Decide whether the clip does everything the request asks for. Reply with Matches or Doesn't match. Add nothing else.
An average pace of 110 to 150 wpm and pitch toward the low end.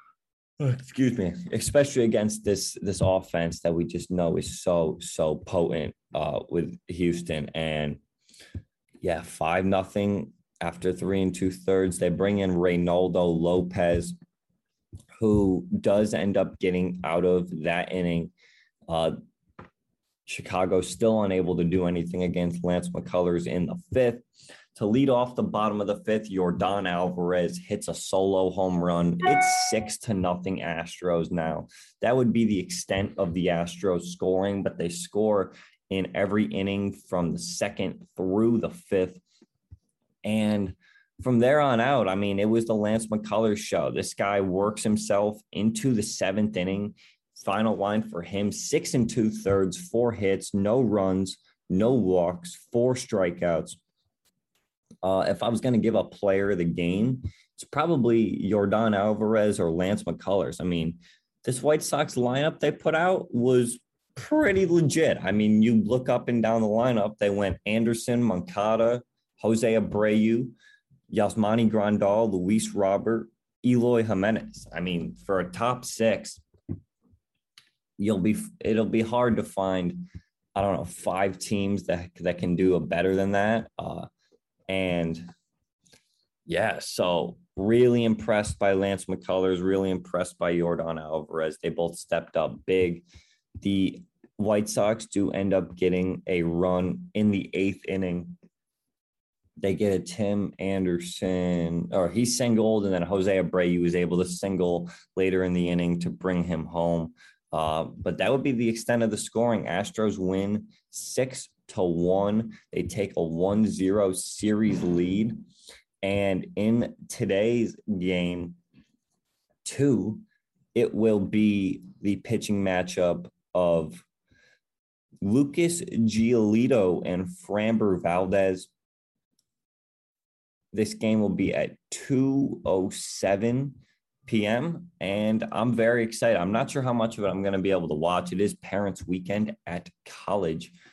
Matches